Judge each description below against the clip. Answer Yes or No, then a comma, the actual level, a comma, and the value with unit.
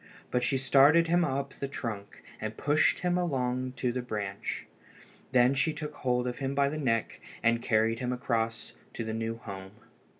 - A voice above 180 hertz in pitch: No, low, 125 Hz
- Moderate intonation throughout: Yes, average, 3.5 semitones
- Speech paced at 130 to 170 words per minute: No, average, 180 wpm